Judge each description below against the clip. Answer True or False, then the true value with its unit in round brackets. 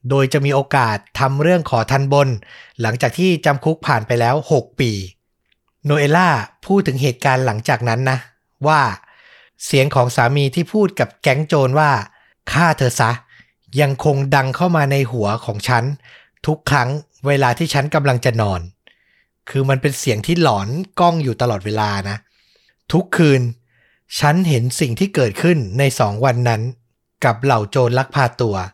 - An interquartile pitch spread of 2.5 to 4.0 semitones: True (3.7 semitones)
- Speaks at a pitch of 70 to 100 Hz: False (135 Hz)